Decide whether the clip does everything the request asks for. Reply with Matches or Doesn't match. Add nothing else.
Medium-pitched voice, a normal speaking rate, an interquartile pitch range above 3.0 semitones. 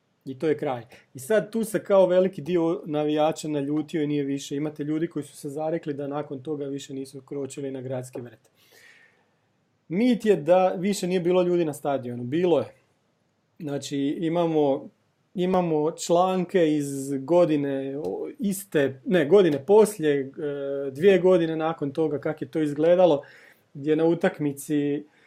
Matches